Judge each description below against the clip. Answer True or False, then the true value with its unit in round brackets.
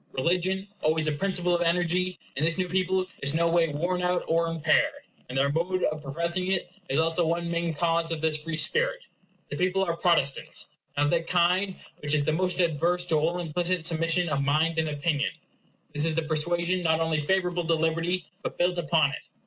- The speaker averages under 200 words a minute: False (205 wpm)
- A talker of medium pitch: True (170 Hz)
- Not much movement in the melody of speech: True (2.2 semitones)